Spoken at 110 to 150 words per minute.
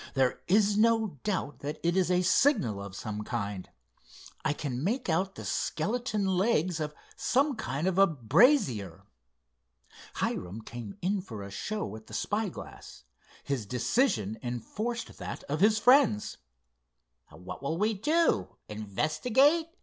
Yes: slow, 135 wpm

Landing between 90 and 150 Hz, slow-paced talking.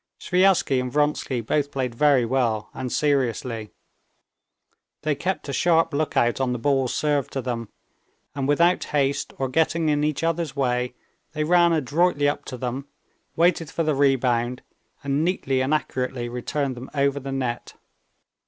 No: medium, 140 Hz; average, 155 wpm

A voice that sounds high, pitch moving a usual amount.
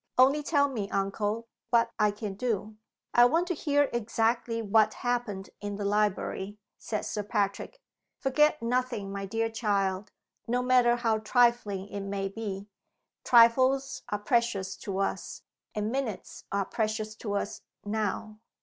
Yes: high, 220 Hz; average, 3.2 semitones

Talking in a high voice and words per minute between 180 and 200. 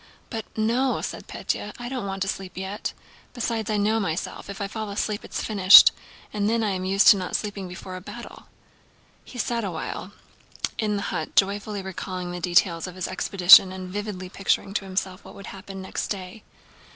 Yes: high, 195 Hz; average, 190 wpm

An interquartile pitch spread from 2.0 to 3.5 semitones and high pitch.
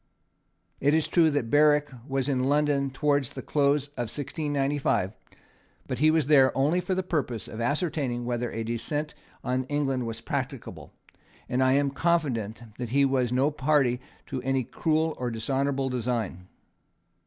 No: average, 3.1 semitones; low, 135 Hz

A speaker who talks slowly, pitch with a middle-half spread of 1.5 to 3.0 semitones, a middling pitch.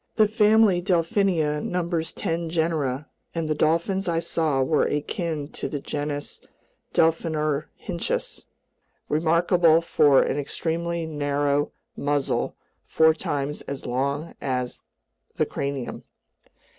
Yes: slow, 105 wpm; average, 2.7 semitones; medium, 160 Hz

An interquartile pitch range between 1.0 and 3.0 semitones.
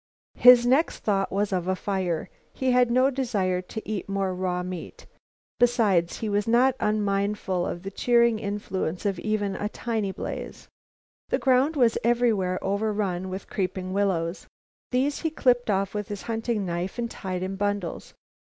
No: average, 4.0 semitones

